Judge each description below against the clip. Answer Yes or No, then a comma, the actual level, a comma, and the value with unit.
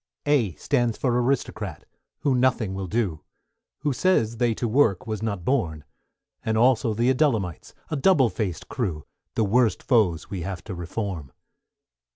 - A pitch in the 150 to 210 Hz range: No, low, 110 Hz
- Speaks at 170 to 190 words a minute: No, average, 155 wpm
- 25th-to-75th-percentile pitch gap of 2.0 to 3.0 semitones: No, average, 4.8 semitones